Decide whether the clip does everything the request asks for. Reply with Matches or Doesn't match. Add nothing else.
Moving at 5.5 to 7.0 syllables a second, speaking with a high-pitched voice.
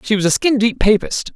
Matches